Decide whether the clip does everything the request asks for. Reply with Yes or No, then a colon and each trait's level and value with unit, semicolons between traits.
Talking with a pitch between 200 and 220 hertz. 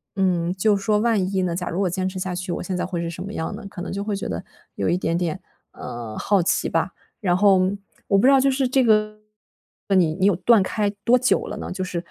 No: high, 190 Hz